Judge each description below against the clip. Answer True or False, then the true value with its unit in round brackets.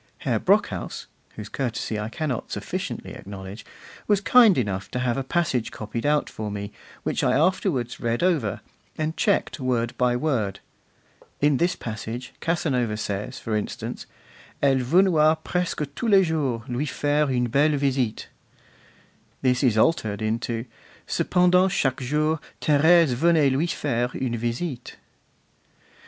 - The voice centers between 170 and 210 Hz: False (130 Hz)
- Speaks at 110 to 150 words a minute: True (140 wpm)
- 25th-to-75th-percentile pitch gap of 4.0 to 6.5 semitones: True (5.3 semitones)